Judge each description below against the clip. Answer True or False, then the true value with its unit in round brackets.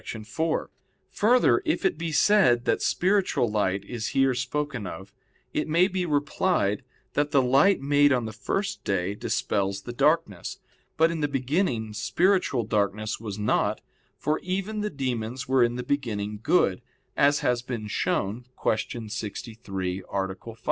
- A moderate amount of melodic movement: False (6.5 semitones)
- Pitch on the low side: True (125 Hz)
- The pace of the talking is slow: False (155 wpm)